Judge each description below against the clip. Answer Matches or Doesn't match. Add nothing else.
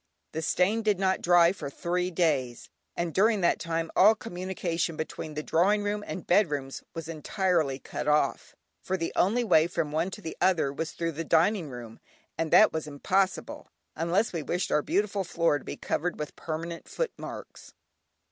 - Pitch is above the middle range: Doesn't match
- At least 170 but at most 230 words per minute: Matches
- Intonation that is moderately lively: Matches